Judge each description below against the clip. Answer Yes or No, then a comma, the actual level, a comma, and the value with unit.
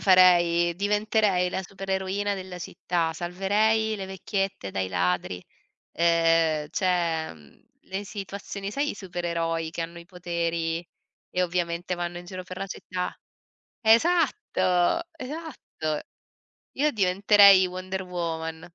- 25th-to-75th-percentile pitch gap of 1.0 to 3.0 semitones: Yes, average, 2.7 semitones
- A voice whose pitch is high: No, medium, 180 Hz